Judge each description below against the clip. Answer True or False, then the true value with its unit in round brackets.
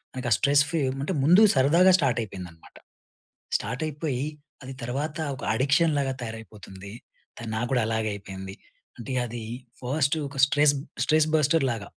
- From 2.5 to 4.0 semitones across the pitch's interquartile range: False (4.8 semitones)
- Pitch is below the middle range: True (130 Hz)